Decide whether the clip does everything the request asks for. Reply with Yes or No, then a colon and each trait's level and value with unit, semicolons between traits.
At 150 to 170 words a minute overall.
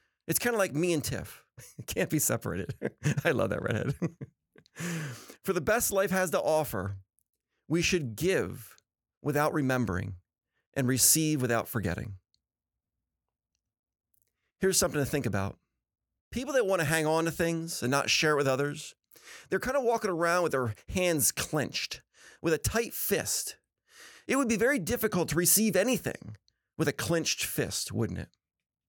Yes: average, 160 wpm